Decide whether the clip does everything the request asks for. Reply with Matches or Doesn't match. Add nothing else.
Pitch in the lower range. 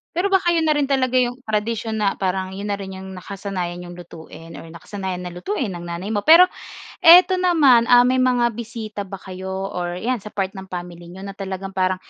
Doesn't match